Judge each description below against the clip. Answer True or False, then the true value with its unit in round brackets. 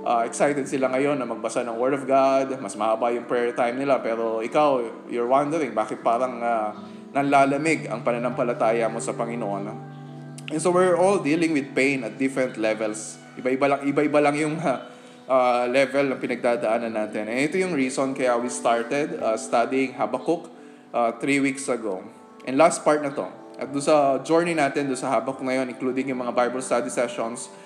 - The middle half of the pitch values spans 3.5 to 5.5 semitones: False (3.0 semitones)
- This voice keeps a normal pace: False (180 wpm)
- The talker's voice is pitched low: True (130 Hz)